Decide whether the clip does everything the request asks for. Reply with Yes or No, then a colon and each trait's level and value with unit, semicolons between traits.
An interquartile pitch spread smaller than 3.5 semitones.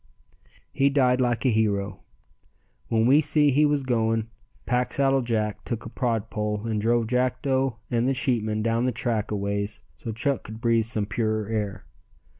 Yes: average, 2.8 semitones